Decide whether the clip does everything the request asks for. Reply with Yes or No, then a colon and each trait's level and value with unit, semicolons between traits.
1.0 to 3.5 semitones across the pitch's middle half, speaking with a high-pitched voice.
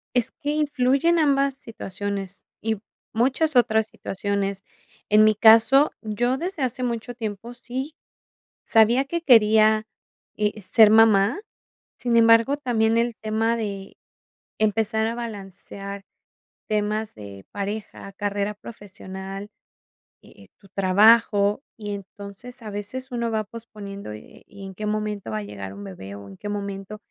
Yes: average, 2.9 semitones; high, 215 Hz